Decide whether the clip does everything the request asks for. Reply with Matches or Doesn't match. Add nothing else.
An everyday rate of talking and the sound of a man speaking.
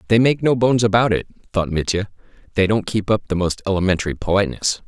Matches